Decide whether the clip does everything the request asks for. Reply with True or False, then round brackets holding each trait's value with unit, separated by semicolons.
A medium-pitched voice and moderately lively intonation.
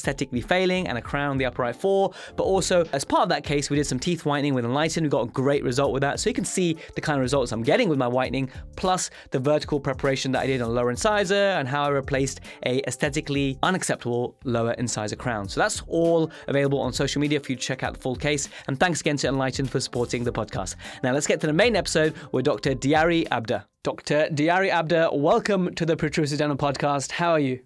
True (145 Hz; 3.5 semitones)